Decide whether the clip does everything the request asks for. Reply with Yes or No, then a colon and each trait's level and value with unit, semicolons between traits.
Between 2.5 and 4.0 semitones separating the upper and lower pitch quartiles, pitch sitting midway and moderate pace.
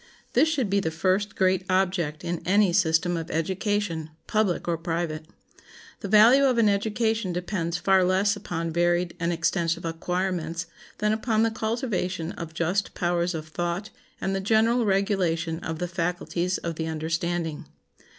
Yes: average, 3.4 semitones; medium, 180 Hz; average, 155 wpm